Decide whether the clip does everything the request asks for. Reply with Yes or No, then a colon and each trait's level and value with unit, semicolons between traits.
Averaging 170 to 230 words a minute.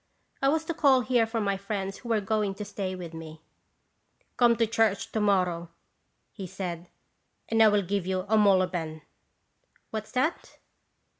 Yes: average, 180 wpm